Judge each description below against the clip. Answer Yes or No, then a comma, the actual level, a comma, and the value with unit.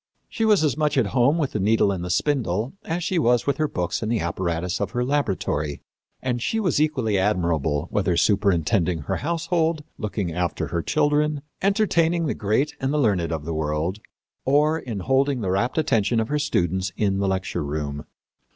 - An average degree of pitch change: No, wide, 8.6 semitones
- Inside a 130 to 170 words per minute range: No, average, 190 wpm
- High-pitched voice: No, low, 115 Hz